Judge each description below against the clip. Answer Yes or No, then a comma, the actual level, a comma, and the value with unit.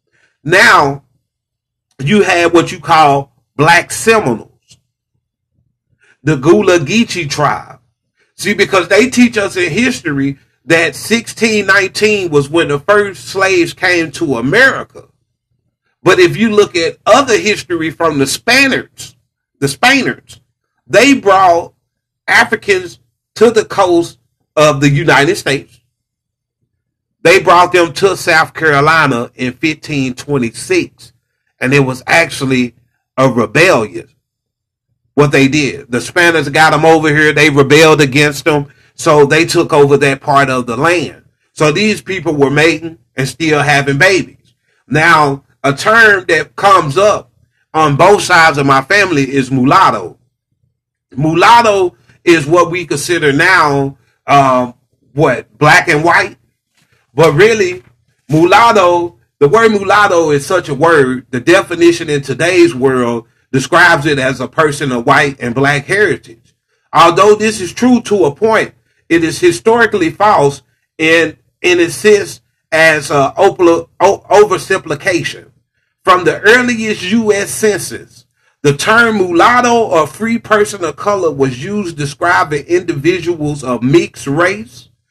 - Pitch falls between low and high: Yes, medium, 155 Hz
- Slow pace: Yes, slow, 130 wpm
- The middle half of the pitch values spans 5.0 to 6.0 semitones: Yes, wide, 5.6 semitones